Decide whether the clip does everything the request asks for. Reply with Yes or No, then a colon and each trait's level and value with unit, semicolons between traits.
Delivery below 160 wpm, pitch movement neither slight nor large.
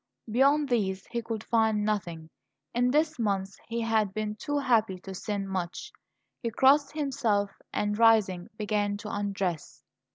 Yes: average, 150 wpm; average, 3.3 semitones